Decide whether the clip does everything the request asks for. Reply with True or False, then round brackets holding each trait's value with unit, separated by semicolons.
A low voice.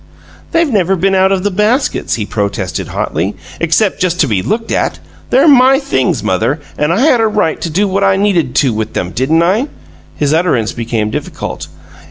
False (175 Hz)